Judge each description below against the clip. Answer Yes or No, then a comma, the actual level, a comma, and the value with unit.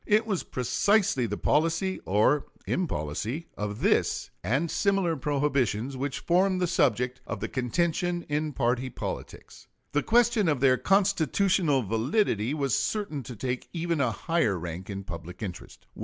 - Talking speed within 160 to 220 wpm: No, average, 140 wpm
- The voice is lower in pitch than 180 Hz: Yes, medium, 140 Hz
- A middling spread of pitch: No, wide, 6.9 semitones